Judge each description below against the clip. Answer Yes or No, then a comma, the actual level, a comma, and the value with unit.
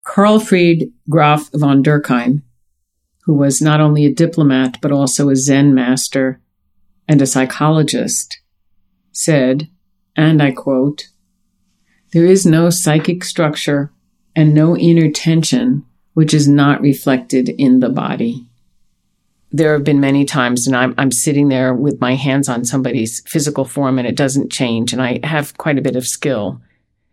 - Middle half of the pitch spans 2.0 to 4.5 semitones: Yes, average, 3.2 semitones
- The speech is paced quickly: No, average, 150 wpm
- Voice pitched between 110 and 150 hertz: Yes, medium, 140 Hz